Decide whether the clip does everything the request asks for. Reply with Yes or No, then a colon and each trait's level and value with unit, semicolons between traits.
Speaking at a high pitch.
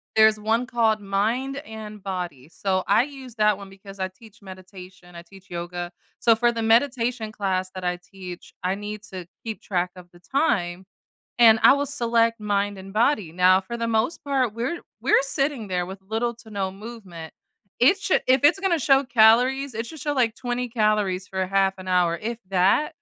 Yes: high, 215 Hz